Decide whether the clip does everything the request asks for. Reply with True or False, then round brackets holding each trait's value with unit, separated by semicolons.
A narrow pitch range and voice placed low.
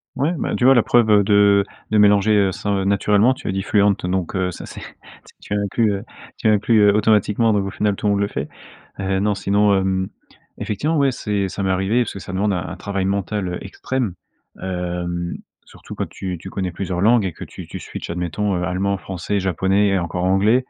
True (1.9 semitones; 100 Hz)